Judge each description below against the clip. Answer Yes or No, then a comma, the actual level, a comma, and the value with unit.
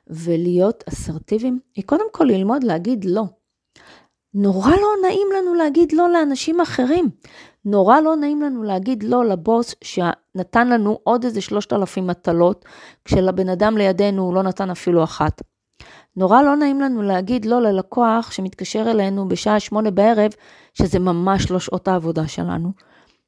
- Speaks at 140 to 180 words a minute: Yes, average, 145 wpm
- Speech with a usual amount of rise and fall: Yes, average, 5.0 semitones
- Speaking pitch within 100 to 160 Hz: No, high, 210 Hz